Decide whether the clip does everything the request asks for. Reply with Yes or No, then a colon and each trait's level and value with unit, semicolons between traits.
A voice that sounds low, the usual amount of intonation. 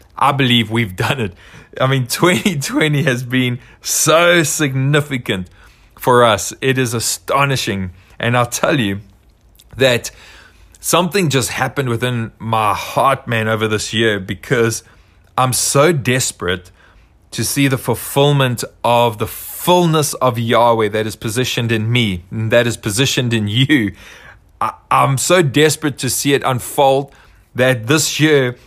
Yes: low, 120 Hz; average, 3.7 semitones